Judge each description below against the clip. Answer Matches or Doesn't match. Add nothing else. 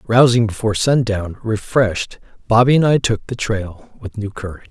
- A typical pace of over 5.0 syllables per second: Matches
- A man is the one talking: Matches